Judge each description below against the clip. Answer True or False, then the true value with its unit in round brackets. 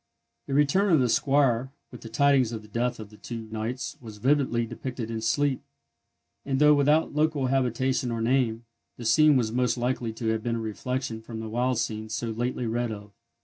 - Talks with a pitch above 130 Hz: False (120 Hz)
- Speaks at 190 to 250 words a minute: True (200 wpm)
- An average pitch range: True (3.0 semitones)